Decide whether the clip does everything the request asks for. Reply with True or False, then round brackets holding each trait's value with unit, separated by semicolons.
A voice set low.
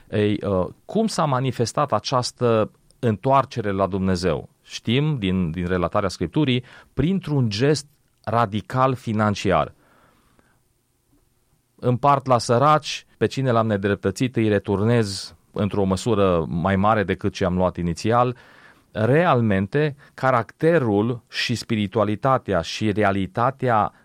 True (115 Hz)